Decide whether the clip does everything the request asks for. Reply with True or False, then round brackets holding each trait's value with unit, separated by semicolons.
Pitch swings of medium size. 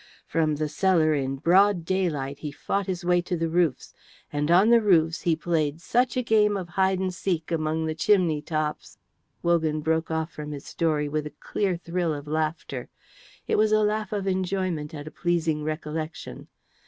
True (3.4 semitones)